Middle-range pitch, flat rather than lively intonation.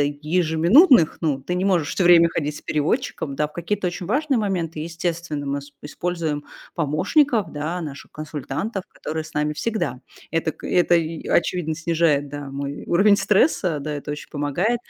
No: medium, 165 Hz; average, 3.5 semitones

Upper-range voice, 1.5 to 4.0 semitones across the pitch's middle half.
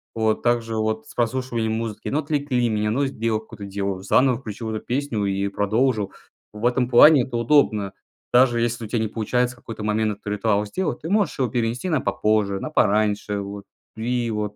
No: low, 115 Hz; average, 2.9 semitones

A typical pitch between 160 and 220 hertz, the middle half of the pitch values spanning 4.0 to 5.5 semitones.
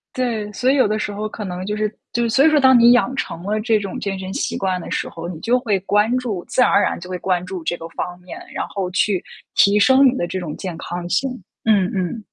Yes: high, 205 Hz; average, 4.4 semitones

